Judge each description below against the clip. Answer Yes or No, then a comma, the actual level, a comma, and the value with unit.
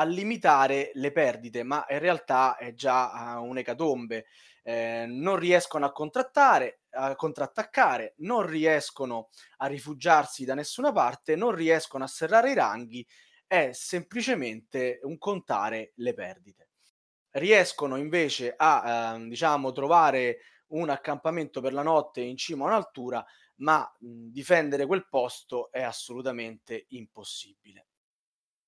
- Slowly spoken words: No, average, 125 wpm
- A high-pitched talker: No, medium, 140 Hz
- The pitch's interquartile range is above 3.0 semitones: Yes, wide, 5.5 semitones